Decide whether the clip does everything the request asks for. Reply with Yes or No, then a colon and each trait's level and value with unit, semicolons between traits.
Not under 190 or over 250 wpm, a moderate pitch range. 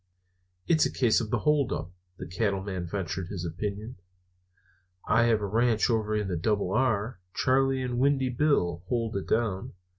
No: average, 160 wpm; average, 4.2 semitones